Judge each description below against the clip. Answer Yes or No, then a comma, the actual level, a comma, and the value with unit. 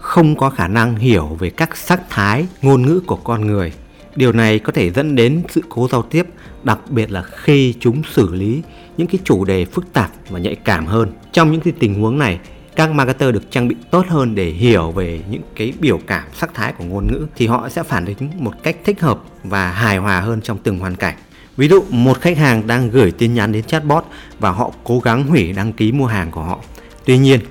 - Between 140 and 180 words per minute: No, average, 235 wpm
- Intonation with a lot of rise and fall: Yes, wide, 6.8 semitones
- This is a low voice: Yes, low, 120 Hz